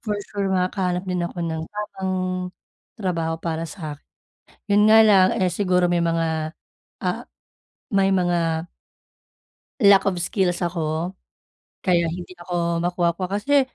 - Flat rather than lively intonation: Yes, narrow, 2.3 semitones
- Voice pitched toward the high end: No, medium, 180 Hz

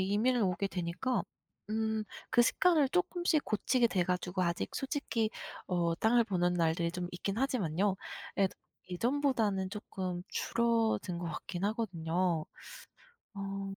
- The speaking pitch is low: No, high, 195 Hz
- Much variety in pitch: No, average, 4.8 semitones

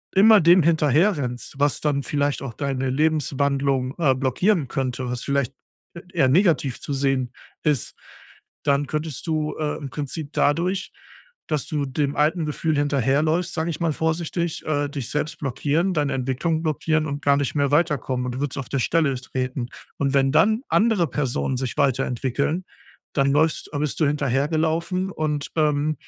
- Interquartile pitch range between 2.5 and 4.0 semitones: Yes, average, 2.8 semitones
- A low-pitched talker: No, medium, 145 Hz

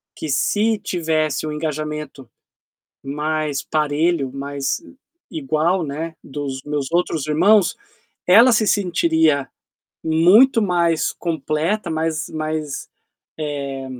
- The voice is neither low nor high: Yes, medium, 155 Hz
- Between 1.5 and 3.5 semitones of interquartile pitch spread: Yes, average, 2.9 semitones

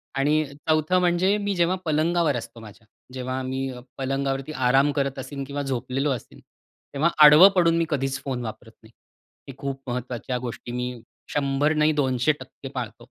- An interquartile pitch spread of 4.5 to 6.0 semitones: No, average, 3.1 semitones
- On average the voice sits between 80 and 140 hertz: Yes, low, 135 Hz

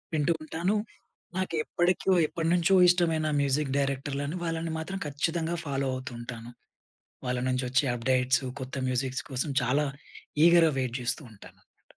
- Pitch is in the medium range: Yes, medium, 145 Hz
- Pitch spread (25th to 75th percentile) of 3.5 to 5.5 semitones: Yes, average, 4.2 semitones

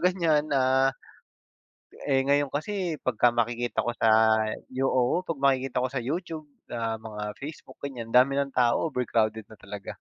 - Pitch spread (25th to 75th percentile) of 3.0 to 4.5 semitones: Yes, average, 3.7 semitones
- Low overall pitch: Yes, low, 130 Hz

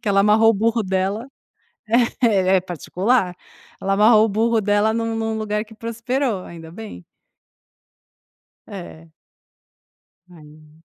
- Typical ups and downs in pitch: Yes, average, 3.3 semitones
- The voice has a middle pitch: No, high, 210 Hz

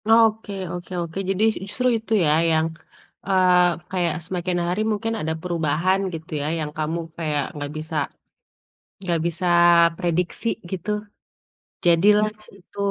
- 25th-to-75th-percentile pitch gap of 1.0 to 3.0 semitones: No, average, 3.4 semitones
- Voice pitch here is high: No, medium, 175 Hz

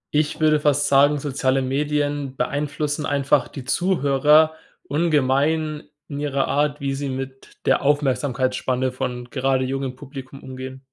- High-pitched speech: No, medium, 140 Hz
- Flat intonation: Yes, narrow, 2.0 semitones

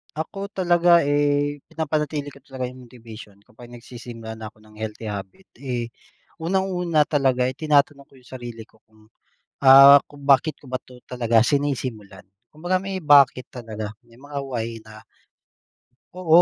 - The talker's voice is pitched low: Yes, low, 130 Hz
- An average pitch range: Yes, average, 4.3 semitones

